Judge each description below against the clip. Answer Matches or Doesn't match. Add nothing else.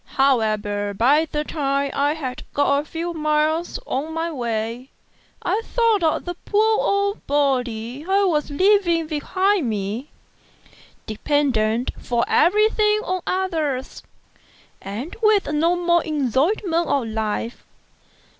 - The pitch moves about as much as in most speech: Doesn't match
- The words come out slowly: Matches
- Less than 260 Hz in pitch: Doesn't match